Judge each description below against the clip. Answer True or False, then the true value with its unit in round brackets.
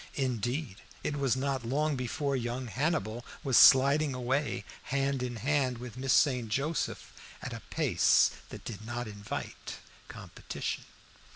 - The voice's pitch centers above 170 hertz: False (130 Hz)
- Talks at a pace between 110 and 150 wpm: True (135 wpm)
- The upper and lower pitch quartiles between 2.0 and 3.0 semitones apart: True (2.6 semitones)